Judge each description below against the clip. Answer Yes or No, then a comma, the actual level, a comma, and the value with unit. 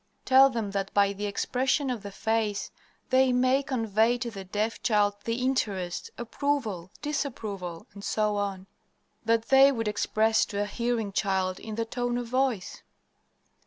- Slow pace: No, average, 150 wpm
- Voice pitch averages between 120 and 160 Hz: No, high, 225 Hz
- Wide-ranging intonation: No, average, 3.7 semitones